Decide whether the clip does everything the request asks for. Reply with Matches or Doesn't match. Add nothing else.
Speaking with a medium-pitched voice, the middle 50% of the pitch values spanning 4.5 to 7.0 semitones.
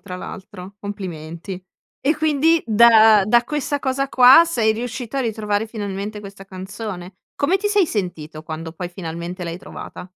Doesn't match